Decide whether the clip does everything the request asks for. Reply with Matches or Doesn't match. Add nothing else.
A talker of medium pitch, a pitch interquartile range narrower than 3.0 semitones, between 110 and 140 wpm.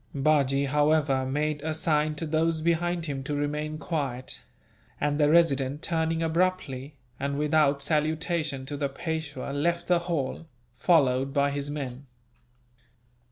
Matches